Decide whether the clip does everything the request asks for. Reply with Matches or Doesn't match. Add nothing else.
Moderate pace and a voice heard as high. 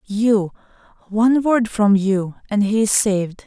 Matches